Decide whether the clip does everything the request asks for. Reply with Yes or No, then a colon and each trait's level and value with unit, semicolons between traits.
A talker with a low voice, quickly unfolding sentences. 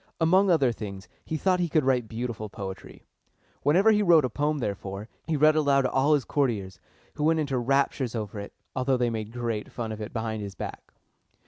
Yes: low, 130 Hz; fast, 210 wpm